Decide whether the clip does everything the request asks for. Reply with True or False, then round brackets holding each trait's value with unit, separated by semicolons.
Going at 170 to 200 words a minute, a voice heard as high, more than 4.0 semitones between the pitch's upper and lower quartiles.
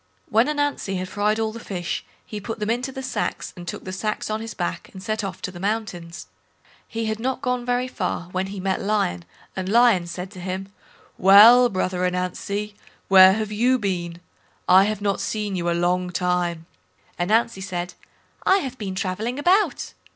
False (190 wpm; 200 Hz; 3.7 semitones)